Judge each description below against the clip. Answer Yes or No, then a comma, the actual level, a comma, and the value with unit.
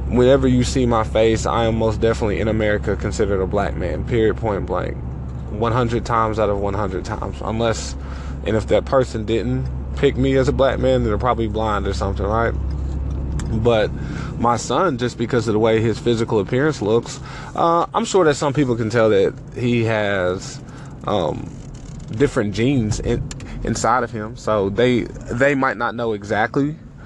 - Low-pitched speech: Yes, low, 115 Hz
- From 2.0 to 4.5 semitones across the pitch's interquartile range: Yes, average, 3.7 semitones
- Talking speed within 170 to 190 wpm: Yes, average, 180 wpm